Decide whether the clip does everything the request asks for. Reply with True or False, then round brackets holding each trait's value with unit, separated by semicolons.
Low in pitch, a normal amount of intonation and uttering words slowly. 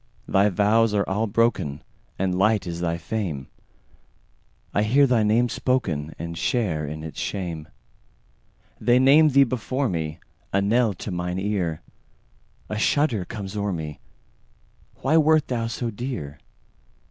False (100 Hz; 5.9 semitones; 115 wpm)